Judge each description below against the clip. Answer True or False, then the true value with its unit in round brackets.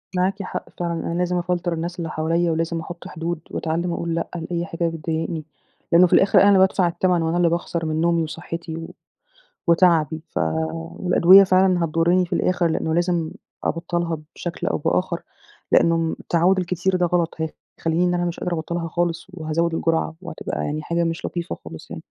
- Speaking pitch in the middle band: True (170 Hz)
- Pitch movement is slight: True (1.4 semitones)